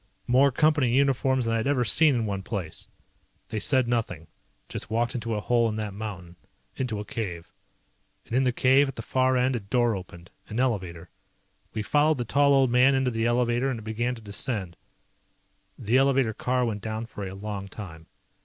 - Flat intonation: No, average, 3.8 semitones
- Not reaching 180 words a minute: No, average, 200 wpm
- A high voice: No, low, 115 Hz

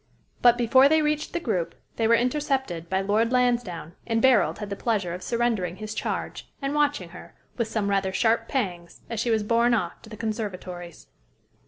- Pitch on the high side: Yes, high, 225 Hz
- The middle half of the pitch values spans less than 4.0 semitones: No, average, 4.3 semitones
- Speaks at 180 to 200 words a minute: Yes, average, 190 wpm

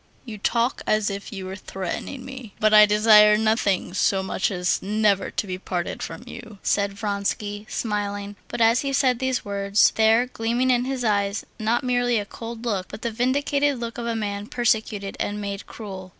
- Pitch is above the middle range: Yes, high, 215 Hz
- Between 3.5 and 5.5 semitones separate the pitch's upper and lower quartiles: No, average, 2.9 semitones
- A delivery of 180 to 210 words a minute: Yes, average, 190 wpm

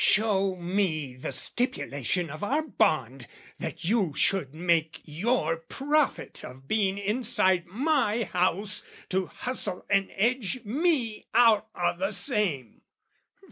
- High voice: Yes, high, 195 Hz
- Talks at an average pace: No, slow, 120 wpm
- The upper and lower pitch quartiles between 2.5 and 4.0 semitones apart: No, wide, 5.5 semitones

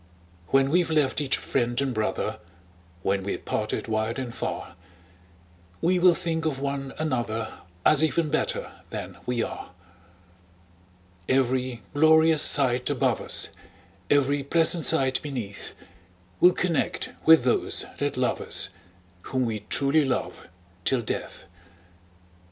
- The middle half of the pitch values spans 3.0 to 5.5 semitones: Yes, average, 4.3 semitones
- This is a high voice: No, low, 135 Hz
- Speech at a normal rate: No, slow, 125 wpm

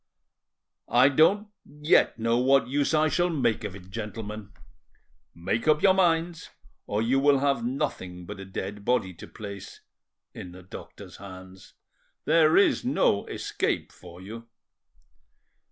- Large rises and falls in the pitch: Yes, wide, 7.3 semitones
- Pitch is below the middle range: Yes, low, 115 Hz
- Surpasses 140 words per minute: No, slow, 135 wpm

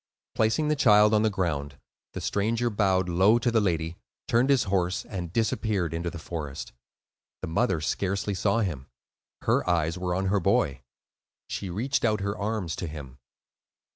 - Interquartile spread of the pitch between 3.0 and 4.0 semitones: No, average, 4.4 semitones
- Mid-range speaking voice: No, very low, 95 Hz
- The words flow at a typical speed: Yes, average, 170 wpm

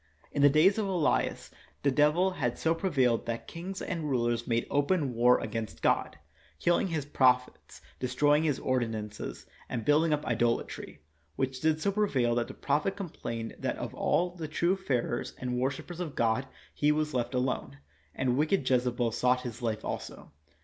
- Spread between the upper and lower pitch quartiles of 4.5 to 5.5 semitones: Yes, average, 4.8 semitones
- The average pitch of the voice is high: No, low, 135 Hz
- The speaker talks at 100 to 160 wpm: No, average, 175 wpm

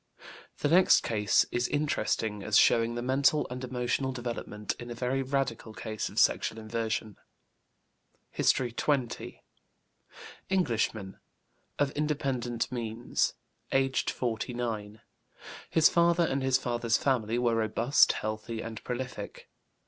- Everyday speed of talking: No, slow, 120 wpm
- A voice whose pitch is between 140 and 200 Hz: No, low, 120 Hz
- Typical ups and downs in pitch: Yes, average, 3.1 semitones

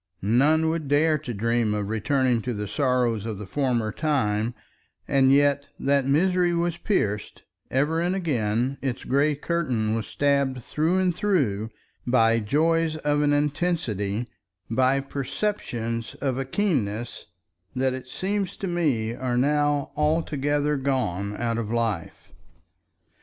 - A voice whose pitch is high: No, low, 135 Hz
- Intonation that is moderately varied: Yes, average, 4.9 semitones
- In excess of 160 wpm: No, slow, 135 wpm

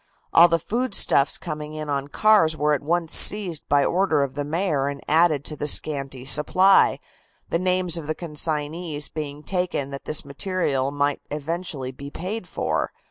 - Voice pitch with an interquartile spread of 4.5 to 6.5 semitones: No, average, 3.5 semitones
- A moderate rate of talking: Yes, average, 175 wpm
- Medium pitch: Yes, medium, 155 Hz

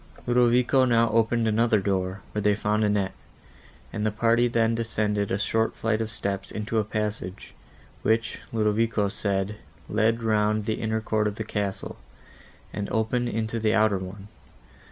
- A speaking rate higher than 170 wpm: No, average, 155 wpm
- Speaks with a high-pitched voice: No, low, 110 Hz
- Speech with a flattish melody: Yes, narrow, 1.6 semitones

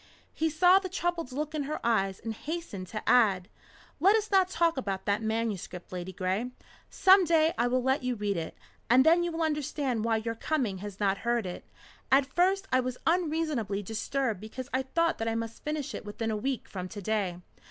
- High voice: Yes, very high, 250 Hz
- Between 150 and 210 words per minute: Yes, fast, 205 wpm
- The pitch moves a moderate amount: No, wide, 7.2 semitones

